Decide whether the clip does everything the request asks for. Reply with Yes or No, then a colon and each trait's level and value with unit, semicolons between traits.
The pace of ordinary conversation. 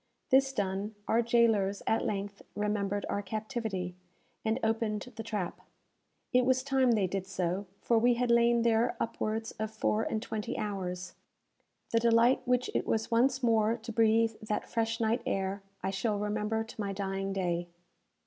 Yes: average, 165 wpm